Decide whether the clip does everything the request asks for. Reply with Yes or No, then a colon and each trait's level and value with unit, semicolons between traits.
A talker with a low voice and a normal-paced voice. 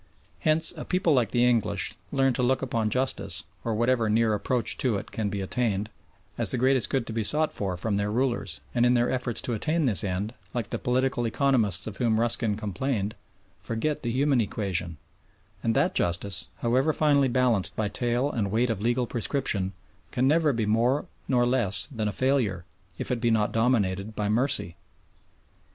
Yes: low, 120 Hz; average, 185 wpm